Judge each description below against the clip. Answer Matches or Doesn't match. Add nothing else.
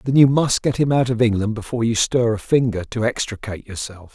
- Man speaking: Matches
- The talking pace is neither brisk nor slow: Doesn't match